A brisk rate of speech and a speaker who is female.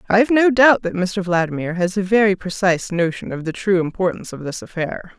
Yes: fast, 210 wpm; female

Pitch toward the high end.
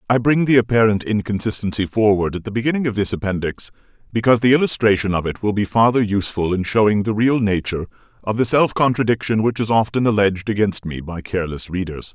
No: low, 105 Hz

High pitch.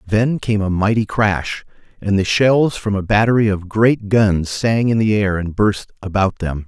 No: low, 105 Hz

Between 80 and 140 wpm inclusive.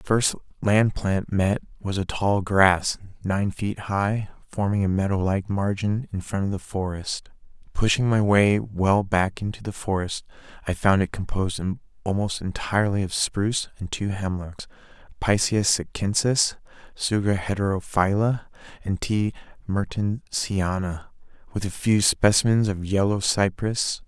Yes: slow, 135 wpm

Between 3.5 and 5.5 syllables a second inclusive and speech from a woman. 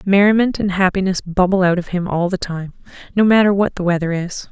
No: 5.8 syllables/s; female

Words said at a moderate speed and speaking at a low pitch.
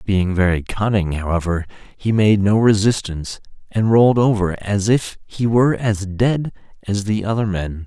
Yes: average, 160 wpm; low, 105 Hz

